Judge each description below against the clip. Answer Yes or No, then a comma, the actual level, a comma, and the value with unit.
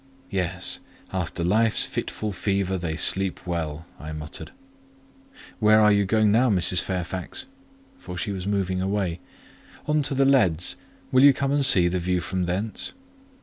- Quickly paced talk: No, average, 150 wpm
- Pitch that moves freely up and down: No, average, 3.3 semitones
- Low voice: Yes, very low, 95 Hz